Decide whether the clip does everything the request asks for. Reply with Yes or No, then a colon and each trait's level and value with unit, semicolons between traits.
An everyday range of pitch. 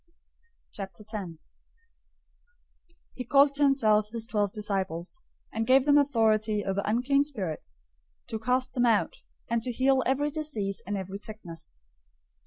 Yes: average, 4.6 semitones